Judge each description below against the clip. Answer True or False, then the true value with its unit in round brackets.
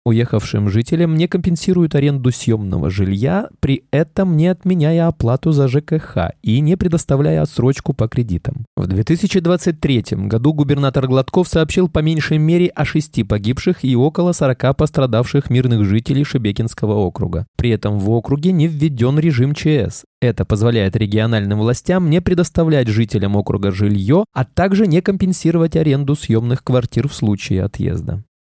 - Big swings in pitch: True (6.4 semitones)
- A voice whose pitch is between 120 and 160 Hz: True (135 Hz)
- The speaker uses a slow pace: False (140 wpm)